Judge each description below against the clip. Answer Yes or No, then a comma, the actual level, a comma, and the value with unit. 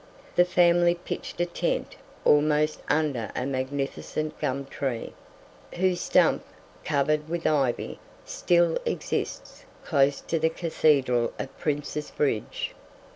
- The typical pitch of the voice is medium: Yes, medium, 150 Hz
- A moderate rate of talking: No, slow, 115 wpm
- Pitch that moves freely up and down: No, average, 3.5 semitones